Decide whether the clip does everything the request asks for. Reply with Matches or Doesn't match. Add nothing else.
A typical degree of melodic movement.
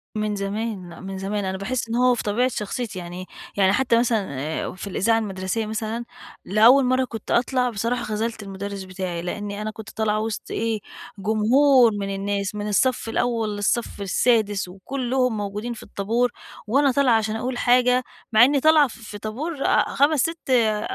Matches